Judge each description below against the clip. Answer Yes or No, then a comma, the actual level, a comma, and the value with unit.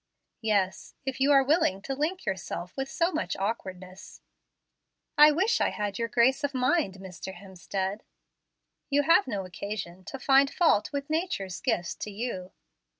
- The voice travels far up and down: Yes, wide, 7.0 semitones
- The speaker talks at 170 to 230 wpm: No, average, 155 wpm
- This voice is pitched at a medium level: No, high, 230 Hz